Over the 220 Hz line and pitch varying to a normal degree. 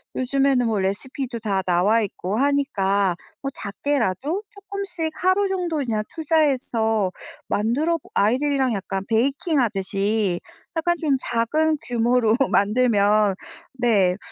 No: high, 240 Hz; wide, 6.0 semitones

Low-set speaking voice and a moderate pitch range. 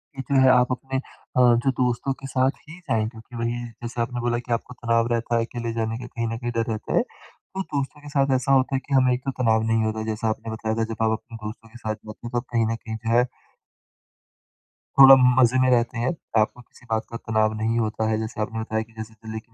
No: low, 115 Hz; narrow, 2.2 semitones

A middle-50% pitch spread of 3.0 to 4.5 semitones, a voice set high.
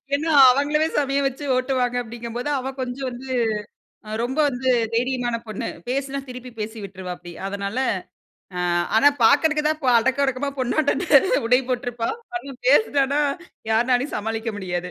Yes: average, 3.3 semitones; very high, 250 Hz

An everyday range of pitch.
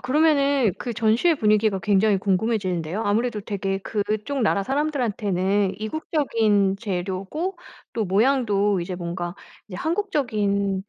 Yes: average, 4.4 semitones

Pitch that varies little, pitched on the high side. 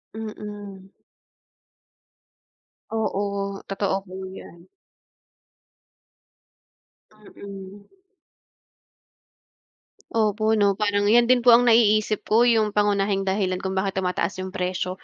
Yes: narrow, 1.9 semitones; high, 205 Hz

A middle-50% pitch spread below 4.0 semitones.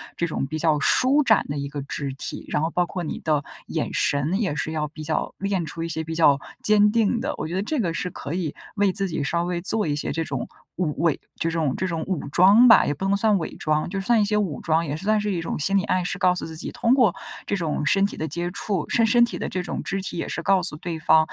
No: average, 4.3 semitones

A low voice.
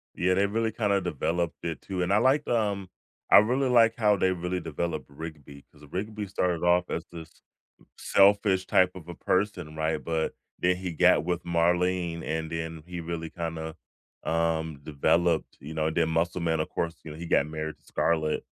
Yes: very low, 85 Hz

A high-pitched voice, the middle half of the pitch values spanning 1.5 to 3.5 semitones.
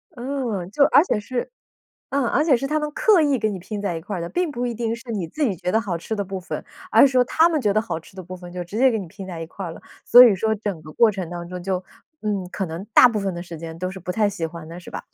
No: high, 205 Hz; average, 5.3 semitones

